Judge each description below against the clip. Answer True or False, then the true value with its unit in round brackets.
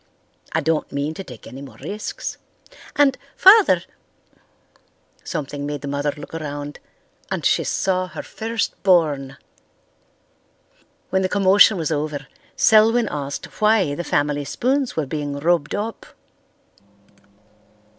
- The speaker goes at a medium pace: False (125 wpm)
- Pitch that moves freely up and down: True (6.0 semitones)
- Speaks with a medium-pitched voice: True (160 Hz)